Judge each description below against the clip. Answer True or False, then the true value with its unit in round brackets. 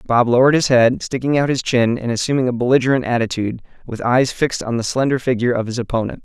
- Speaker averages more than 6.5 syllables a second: True (6.8 syllables/s)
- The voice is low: True (125 Hz)